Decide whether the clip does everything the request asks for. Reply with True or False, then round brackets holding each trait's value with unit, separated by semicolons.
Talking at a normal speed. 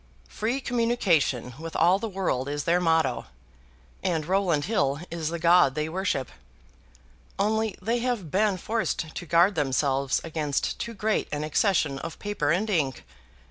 True (150 wpm)